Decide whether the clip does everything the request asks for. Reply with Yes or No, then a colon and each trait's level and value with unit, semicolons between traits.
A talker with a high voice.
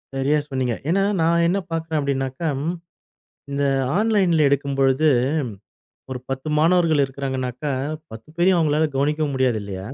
No: medium, 140 Hz